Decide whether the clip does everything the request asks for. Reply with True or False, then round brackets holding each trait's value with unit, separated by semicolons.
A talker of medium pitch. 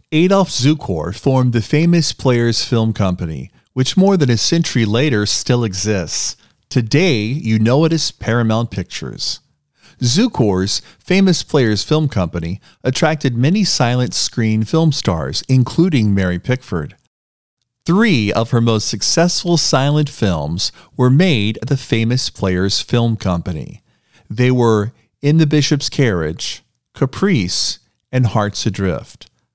False (120 Hz)